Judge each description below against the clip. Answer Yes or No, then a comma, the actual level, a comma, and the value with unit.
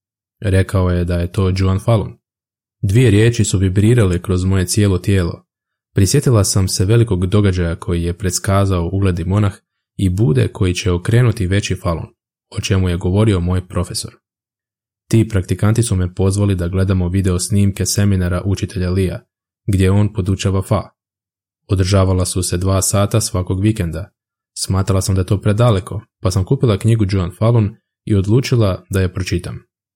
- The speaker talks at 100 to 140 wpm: No, average, 155 wpm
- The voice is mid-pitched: No, very low, 95 Hz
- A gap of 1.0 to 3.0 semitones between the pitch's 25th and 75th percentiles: Yes, narrow, 2.5 semitones